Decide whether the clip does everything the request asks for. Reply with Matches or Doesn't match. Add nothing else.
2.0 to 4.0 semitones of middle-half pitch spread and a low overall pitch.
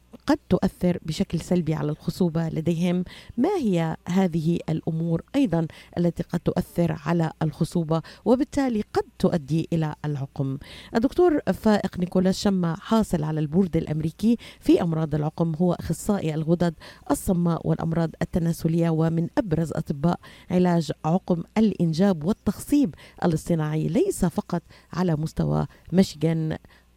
Doesn't match